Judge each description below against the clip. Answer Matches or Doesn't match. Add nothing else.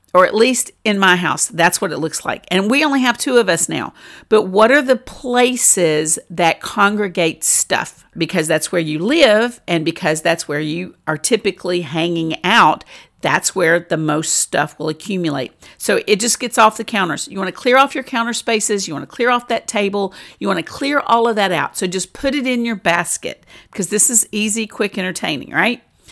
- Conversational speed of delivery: Doesn't match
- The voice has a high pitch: Matches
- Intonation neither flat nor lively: Doesn't match